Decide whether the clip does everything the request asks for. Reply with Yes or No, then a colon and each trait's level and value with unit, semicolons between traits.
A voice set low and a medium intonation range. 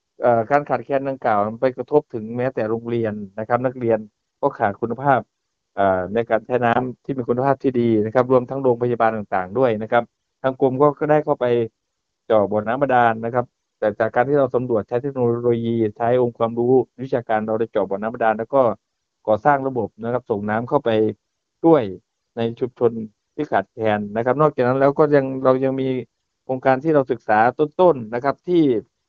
Yes: low, 120 Hz; average, 3.1 semitones